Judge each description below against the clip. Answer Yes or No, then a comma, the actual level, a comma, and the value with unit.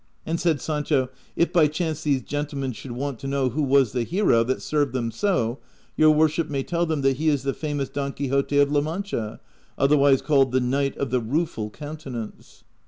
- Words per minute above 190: Yes, average, 200 wpm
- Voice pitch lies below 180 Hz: Yes, medium, 140 Hz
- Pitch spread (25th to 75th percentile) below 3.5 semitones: Yes, average, 2.8 semitones